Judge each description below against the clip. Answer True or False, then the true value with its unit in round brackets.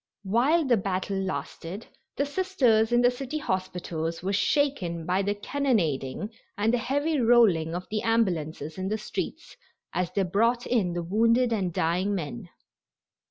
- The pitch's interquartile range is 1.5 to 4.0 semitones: False (5.2 semitones)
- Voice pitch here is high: True (205 Hz)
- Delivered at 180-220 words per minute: False (155 wpm)